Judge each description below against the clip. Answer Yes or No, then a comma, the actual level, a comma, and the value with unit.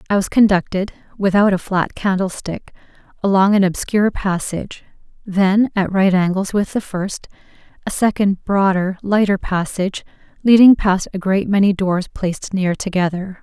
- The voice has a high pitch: Yes, high, 195 Hz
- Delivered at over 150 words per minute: No, average, 145 wpm